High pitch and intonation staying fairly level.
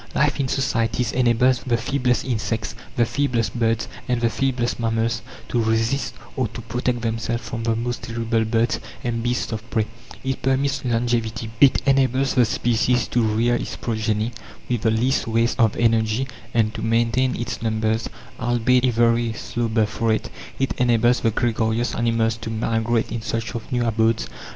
No: low, 115 Hz; narrow, 1.5 semitones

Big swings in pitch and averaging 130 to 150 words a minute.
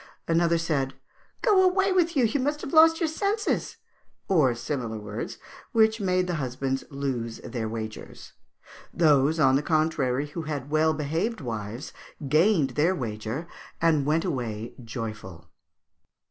Yes: wide, 6.8 semitones; average, 140 wpm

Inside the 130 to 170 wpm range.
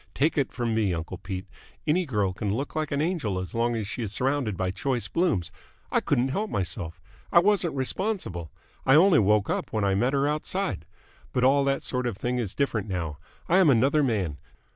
No: fast, 205 wpm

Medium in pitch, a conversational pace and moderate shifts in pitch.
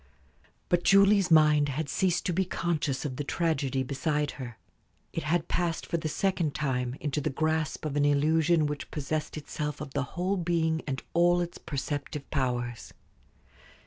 Yes: medium, 155 Hz; average, 165 wpm; average, 3.2 semitones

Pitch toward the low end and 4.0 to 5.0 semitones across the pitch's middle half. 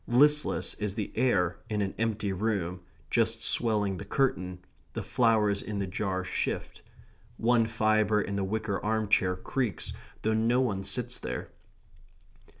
No: low, 105 Hz; average, 2.7 semitones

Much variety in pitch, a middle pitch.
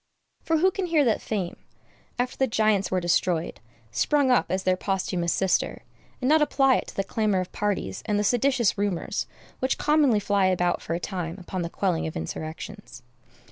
No: wide, 5.9 semitones; high, 200 Hz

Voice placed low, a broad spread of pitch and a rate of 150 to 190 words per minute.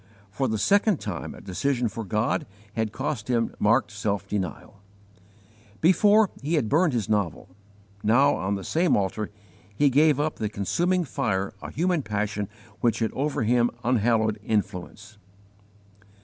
Yes: low, 115 Hz; wide, 5.8 semitones; average, 155 wpm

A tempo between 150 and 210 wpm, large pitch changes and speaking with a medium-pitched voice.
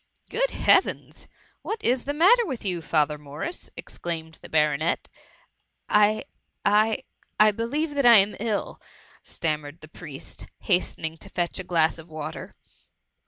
Yes: average, 155 wpm; wide, 6.7 semitones; medium, 180 Hz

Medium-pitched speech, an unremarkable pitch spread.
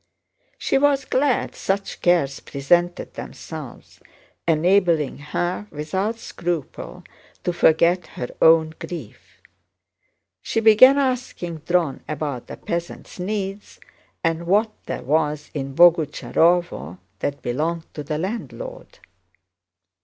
Yes: medium, 170 Hz; average, 4.6 semitones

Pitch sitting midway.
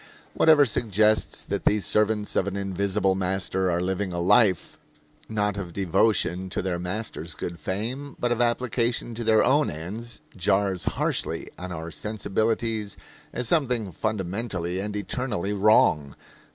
No: low, 100 Hz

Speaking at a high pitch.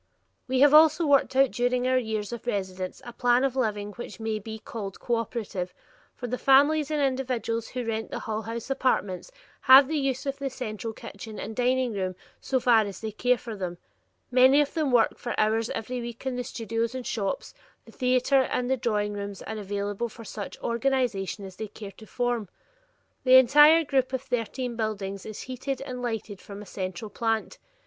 Yes: high, 235 Hz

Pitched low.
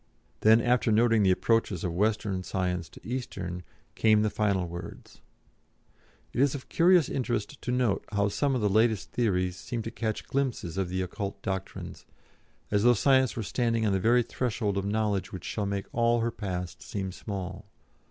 Yes: low, 105 Hz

